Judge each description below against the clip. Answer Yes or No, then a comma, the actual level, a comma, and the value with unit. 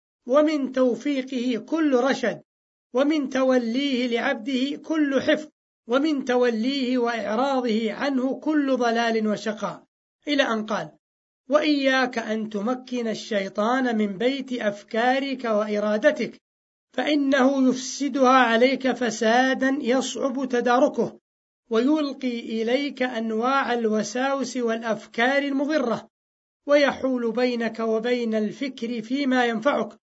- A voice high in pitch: Yes, very high, 250 Hz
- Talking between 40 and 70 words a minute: No, average, 90 wpm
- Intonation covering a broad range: No, average, 2.9 semitones